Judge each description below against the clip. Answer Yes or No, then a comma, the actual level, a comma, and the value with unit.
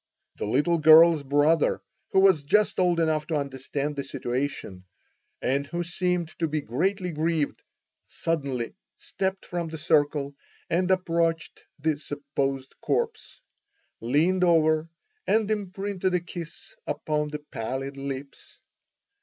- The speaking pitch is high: No, medium, 155 Hz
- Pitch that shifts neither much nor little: Yes, average, 3.8 semitones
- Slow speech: Yes, slow, 125 wpm